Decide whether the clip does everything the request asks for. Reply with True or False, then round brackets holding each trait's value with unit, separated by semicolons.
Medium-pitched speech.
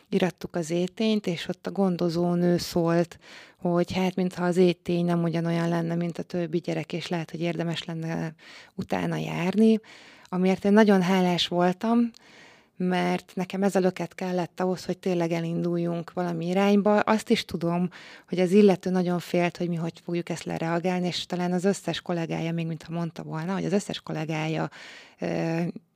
True (175 Hz)